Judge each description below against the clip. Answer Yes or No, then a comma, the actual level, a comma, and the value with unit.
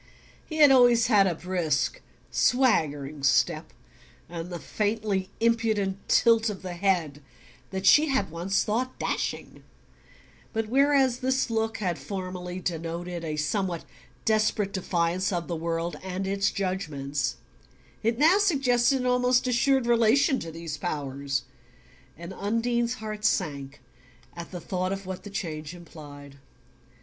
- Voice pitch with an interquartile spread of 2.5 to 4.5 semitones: No, wide, 5.6 semitones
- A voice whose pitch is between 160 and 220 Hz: Yes, high, 190 Hz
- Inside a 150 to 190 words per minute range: No, slow, 135 wpm